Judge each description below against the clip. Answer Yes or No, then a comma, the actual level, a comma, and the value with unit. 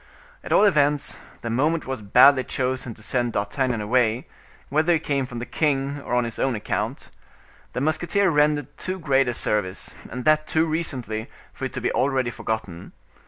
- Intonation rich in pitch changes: No, average, 4.2 semitones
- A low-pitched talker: Yes, low, 130 Hz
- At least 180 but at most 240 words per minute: Yes, average, 185 wpm